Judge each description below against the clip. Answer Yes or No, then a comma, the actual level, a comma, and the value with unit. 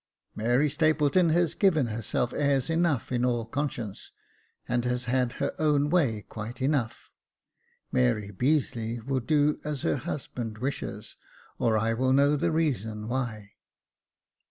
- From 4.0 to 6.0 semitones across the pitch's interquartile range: Yes, average, 4.5 semitones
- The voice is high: No, low, 130 Hz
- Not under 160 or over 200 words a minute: No, average, 140 wpm